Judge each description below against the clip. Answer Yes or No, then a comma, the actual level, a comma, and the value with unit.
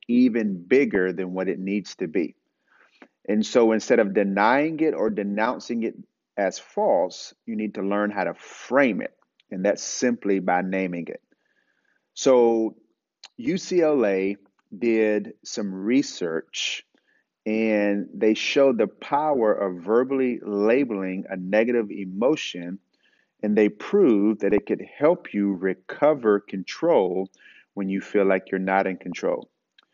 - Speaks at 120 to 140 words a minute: Yes, slow, 135 wpm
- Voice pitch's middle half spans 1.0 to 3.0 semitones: Yes, average, 2.7 semitones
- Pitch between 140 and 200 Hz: No, low, 105 Hz